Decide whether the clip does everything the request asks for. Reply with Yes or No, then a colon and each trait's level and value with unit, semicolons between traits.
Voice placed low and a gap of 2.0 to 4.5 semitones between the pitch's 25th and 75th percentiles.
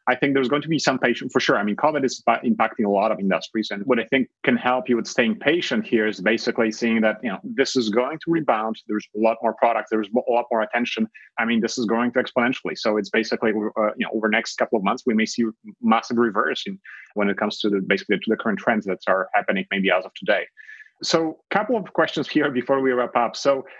Yes: low, 120 Hz; average, 3.8 semitones